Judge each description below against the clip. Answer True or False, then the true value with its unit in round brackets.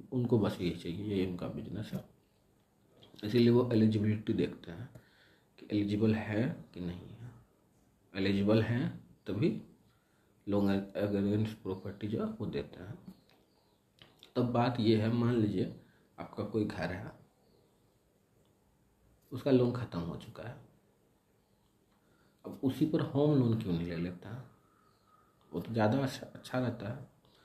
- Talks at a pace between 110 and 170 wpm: True (140 wpm)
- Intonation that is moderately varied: True (3.8 semitones)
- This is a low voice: True (110 Hz)